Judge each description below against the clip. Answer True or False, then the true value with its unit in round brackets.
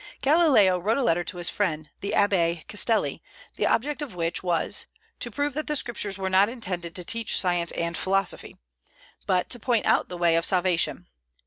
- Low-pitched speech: False (190 Hz)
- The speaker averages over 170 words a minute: True (190 wpm)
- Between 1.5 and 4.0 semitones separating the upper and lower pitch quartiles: False (4.9 semitones)